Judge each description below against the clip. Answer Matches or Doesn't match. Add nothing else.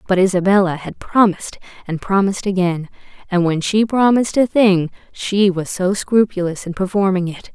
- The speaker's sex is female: Matches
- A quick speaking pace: Doesn't match